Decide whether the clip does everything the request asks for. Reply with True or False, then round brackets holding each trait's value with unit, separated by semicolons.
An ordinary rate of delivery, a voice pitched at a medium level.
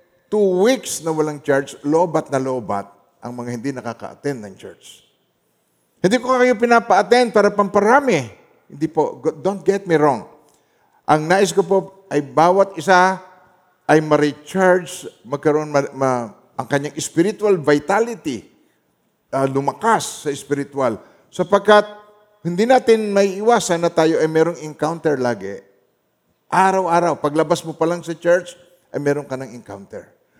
True (135 wpm; 165 Hz)